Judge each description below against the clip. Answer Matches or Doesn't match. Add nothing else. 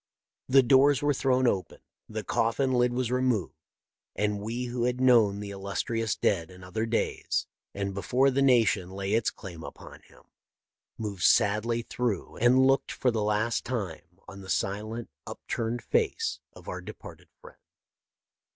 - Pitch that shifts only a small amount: Doesn't match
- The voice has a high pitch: Doesn't match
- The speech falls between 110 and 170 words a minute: Matches